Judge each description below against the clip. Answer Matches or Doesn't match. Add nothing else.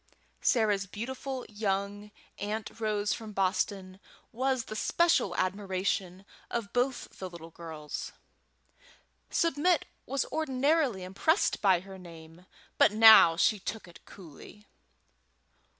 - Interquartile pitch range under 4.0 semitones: Doesn't match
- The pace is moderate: Doesn't match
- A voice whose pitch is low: Doesn't match